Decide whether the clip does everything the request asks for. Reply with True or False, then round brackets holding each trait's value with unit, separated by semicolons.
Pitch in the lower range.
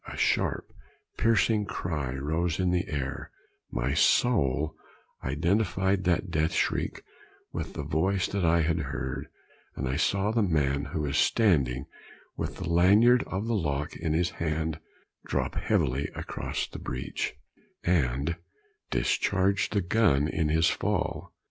True (80 Hz)